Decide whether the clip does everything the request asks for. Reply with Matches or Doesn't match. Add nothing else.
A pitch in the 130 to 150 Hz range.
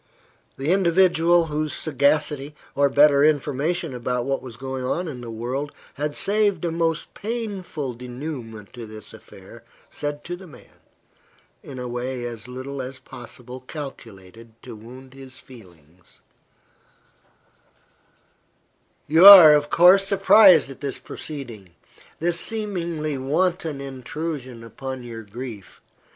Matches